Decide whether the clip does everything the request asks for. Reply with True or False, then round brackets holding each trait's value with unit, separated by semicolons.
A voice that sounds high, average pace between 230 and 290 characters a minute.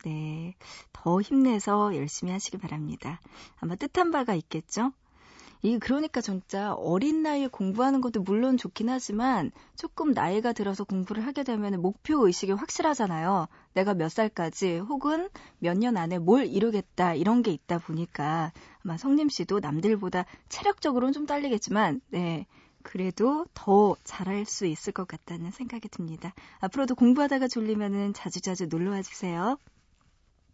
False (205 Hz; 325 characters per minute)